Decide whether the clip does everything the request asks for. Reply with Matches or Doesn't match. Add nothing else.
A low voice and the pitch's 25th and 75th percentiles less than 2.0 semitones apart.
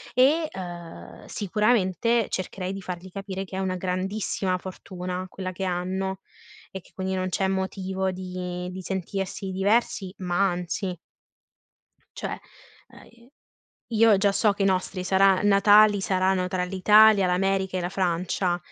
Doesn't match